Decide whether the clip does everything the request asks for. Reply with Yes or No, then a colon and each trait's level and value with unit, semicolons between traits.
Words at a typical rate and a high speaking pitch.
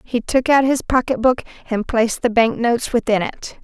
No: fast, 215 wpm; high, 240 Hz